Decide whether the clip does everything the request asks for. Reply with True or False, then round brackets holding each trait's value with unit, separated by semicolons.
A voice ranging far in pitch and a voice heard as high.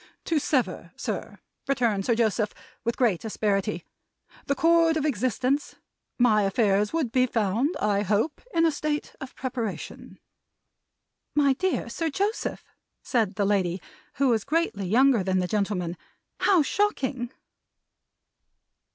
True (5.9 semitones; 240 Hz)